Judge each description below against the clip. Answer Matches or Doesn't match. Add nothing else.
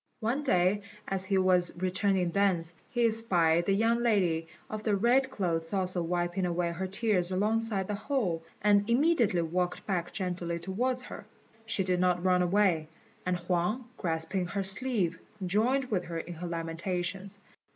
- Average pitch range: Matches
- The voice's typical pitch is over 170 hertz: Matches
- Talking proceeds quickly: Doesn't match